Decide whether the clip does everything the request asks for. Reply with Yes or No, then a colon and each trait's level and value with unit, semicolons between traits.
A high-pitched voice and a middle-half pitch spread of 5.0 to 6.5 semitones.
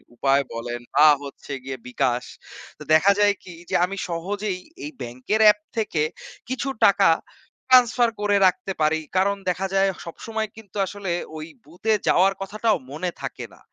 Yes: high, 195 Hz; average, 5.3 semitones